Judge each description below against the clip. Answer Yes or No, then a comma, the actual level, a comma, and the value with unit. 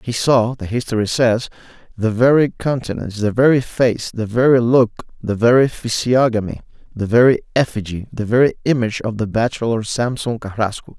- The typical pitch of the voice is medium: No, low, 115 Hz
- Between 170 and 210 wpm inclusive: No, average, 155 wpm